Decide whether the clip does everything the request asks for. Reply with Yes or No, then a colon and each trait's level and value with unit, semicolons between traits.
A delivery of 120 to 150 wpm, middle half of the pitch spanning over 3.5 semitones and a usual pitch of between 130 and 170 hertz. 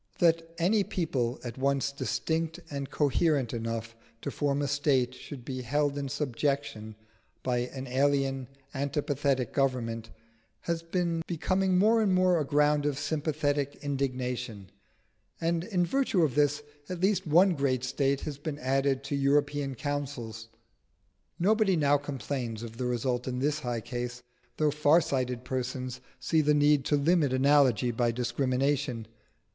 No: average, 145 wpm; average, 3.1 semitones; medium, 140 Hz